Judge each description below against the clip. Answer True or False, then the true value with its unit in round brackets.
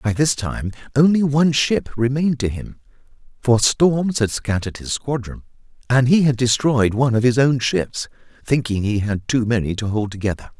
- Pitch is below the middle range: True (125 Hz)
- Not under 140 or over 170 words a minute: False (180 wpm)